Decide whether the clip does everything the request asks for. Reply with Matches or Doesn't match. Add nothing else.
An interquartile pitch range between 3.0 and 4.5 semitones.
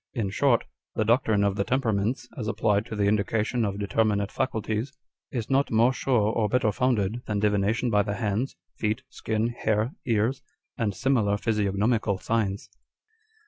Doesn't match